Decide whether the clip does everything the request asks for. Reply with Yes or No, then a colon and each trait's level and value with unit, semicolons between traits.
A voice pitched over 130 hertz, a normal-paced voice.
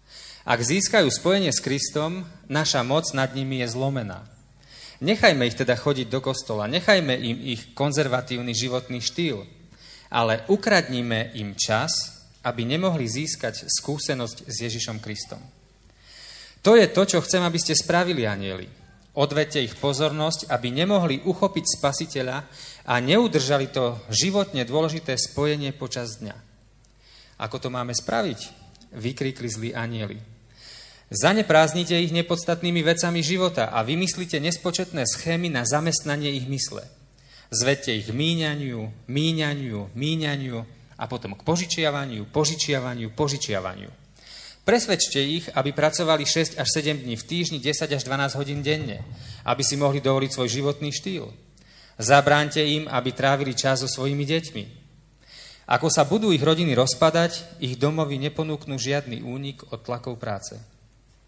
Yes: medium, 140 Hz; average, 130 wpm